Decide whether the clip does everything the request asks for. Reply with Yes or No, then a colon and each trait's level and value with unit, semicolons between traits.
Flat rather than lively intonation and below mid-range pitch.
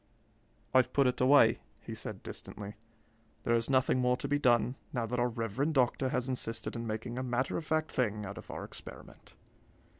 Yes: narrow, 2.2 semitones; low, 125 Hz